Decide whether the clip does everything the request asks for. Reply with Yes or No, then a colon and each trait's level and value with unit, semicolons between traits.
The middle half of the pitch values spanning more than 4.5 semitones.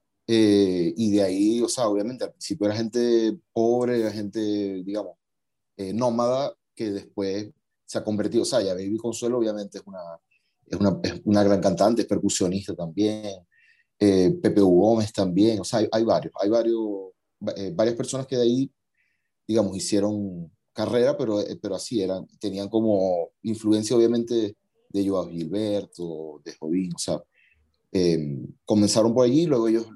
No: average, 2.8 semitones